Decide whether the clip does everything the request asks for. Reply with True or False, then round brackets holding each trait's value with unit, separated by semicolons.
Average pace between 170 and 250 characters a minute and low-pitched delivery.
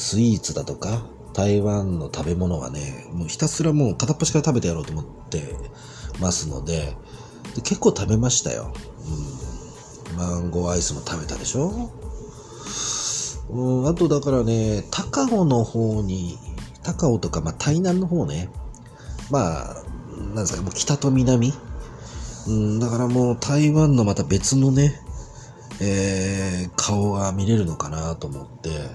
False (280 characters per minute; 105 Hz)